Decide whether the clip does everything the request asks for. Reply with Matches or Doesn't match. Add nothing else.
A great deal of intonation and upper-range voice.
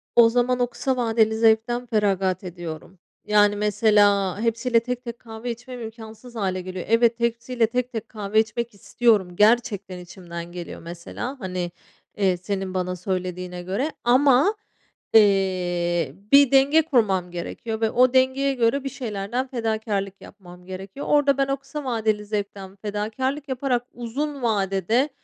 Doesn't match